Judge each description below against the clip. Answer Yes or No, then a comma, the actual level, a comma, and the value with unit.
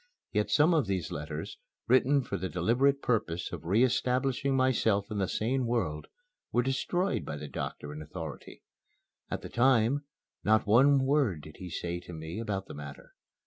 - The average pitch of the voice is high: No, low, 110 Hz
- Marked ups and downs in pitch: Yes, wide, 7.4 semitones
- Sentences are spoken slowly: No, average, 175 wpm